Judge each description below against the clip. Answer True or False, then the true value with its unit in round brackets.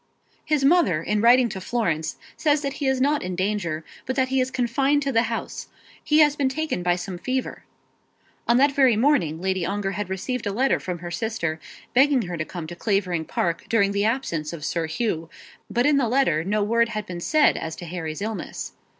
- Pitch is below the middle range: False (215 Hz)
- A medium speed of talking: False (210 wpm)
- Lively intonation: True (7.0 semitones)